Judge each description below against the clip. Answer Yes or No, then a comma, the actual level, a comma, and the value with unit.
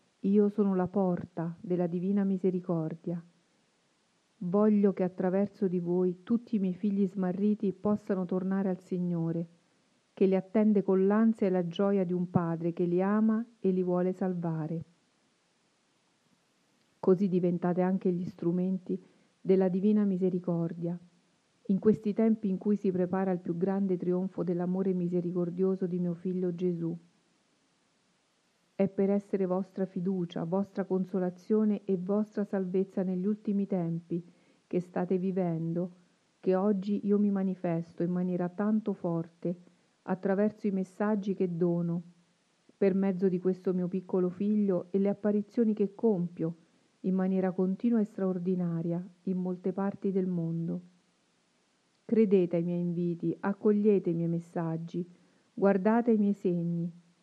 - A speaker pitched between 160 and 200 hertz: Yes, medium, 185 Hz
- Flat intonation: Yes, narrow, 2.0 semitones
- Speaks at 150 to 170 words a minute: No, average, 135 wpm